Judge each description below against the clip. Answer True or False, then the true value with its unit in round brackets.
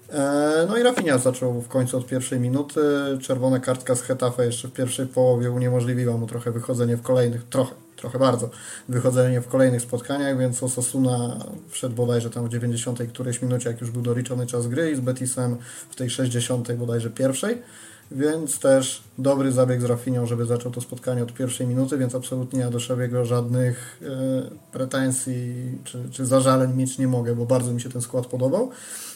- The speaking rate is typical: False (180 wpm)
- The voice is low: True (125 Hz)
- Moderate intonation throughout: False (1.2 semitones)